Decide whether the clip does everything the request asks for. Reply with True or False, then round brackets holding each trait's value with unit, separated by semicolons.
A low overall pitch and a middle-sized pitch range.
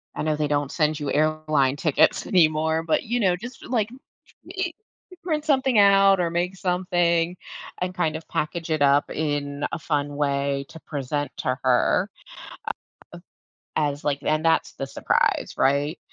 False (155 Hz; 3.8 semitones)